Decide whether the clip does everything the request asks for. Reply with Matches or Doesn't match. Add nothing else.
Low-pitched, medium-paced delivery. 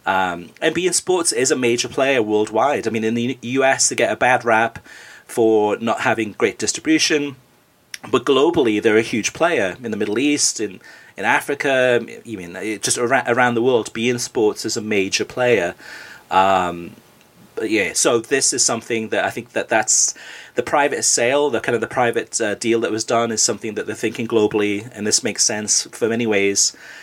Matches